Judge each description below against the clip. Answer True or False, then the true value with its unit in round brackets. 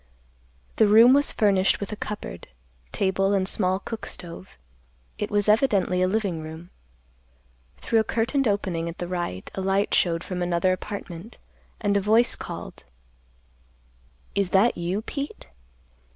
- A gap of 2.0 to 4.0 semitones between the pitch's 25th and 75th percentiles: True (3.0 semitones)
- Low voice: False (195 Hz)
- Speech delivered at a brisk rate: False (145 wpm)